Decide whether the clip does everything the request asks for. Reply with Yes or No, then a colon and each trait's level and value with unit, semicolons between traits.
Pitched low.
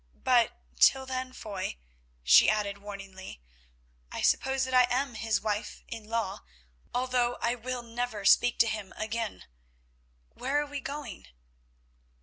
No: high, 235 Hz